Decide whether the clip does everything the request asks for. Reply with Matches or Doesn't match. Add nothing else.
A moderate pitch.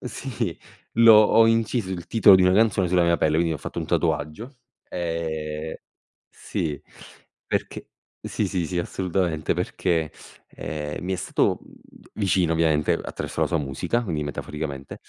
Doesn't match